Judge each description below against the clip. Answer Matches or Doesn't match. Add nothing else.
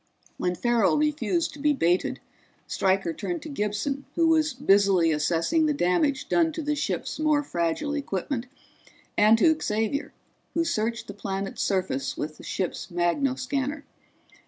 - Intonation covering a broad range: Matches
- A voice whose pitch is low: Doesn't match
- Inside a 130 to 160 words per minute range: Matches